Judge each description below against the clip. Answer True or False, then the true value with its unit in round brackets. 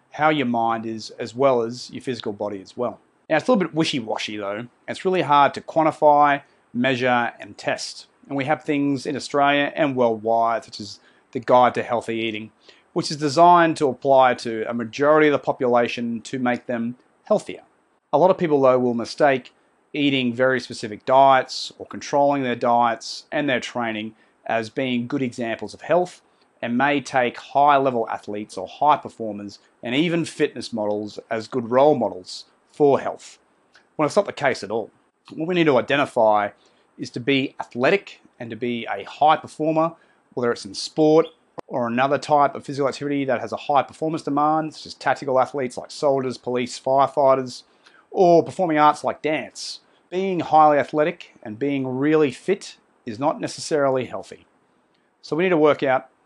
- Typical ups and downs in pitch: True (4.0 semitones)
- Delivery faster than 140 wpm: True (180 wpm)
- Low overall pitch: True (130 Hz)